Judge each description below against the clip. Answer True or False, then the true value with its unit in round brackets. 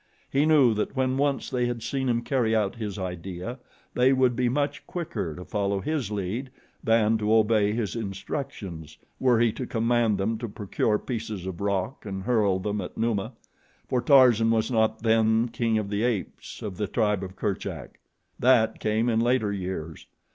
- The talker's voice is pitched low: True (110 Hz)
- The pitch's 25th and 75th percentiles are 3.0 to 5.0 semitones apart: True (3.3 semitones)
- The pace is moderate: True (180 wpm)